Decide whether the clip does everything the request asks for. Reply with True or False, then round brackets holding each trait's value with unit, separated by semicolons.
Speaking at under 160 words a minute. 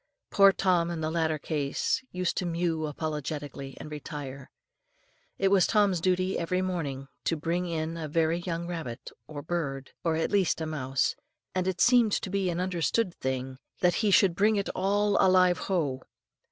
False (175 wpm)